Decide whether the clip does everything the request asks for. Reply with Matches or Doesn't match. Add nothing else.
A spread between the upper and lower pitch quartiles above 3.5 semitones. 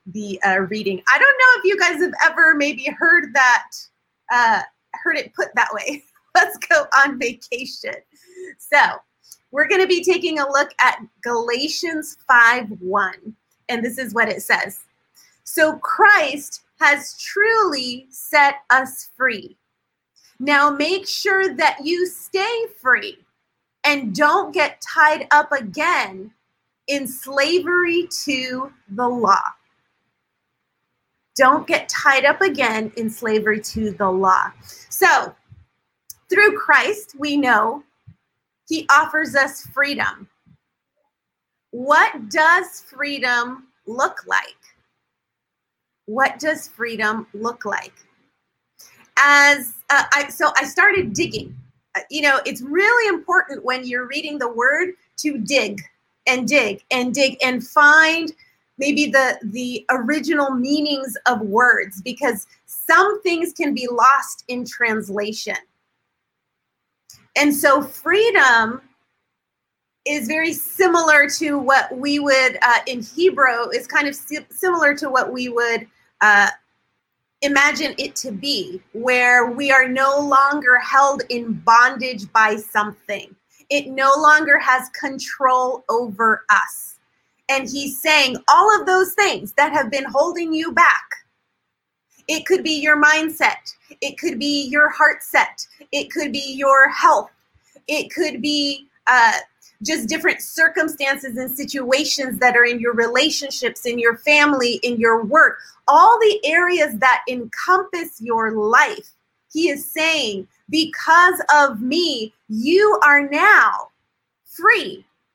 Matches